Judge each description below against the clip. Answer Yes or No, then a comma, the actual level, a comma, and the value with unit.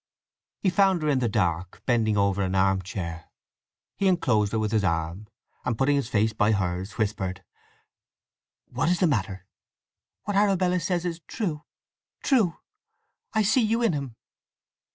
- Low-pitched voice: Yes, low, 115 Hz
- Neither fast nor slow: Yes, average, 150 wpm